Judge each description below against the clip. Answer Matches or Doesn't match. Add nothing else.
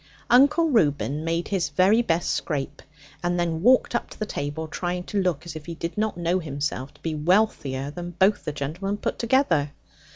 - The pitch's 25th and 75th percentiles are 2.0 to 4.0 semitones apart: Doesn't match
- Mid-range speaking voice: Matches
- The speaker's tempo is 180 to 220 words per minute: Matches